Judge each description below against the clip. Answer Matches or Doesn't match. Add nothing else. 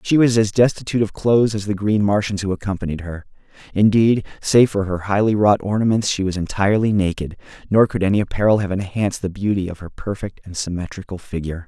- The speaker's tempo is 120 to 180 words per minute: Doesn't match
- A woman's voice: Doesn't match